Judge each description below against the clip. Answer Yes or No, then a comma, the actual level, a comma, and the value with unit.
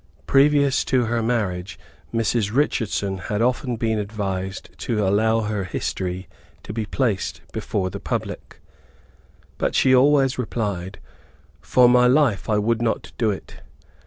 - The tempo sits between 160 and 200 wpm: No, slow, 135 wpm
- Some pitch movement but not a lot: Yes, average, 3.7 semitones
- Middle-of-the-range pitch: No, low, 110 Hz